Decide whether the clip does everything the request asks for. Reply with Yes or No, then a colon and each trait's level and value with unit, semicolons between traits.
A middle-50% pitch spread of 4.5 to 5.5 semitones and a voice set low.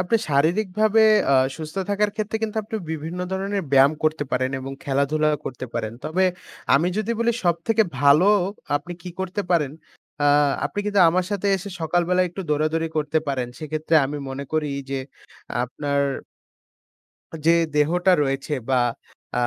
No: average, 4.8 semitones; medium, 160 Hz